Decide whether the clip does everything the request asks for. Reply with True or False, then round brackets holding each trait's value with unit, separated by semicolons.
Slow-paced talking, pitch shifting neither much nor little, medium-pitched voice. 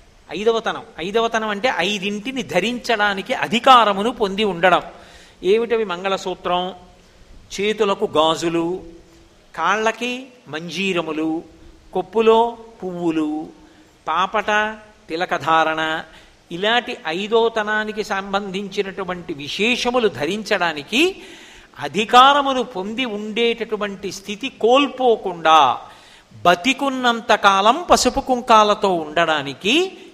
False (65 wpm; 4.7 semitones; 210 Hz)